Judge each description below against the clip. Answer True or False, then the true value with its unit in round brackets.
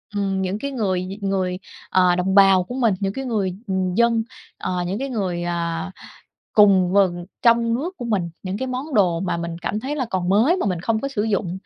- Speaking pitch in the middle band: False (195 Hz)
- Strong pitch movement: False (4.1 semitones)